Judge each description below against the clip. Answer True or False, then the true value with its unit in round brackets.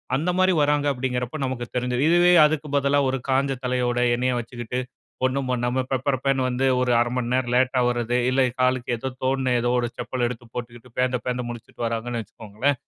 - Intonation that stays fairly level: True (1.6 semitones)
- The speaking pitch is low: True (125 Hz)